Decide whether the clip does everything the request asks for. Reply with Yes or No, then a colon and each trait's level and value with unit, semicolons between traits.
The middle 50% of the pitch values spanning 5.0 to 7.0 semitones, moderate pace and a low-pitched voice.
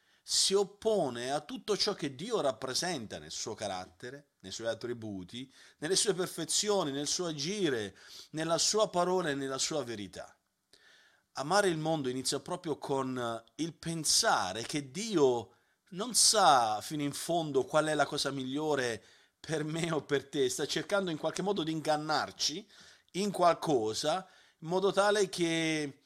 No: wide, 5.4 semitones; average, 150 wpm; medium, 155 Hz